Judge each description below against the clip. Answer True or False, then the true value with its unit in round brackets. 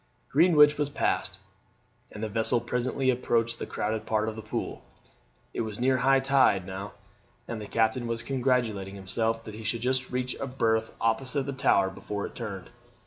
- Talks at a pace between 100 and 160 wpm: False (180 wpm)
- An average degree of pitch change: True (3.2 semitones)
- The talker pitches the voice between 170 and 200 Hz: False (115 Hz)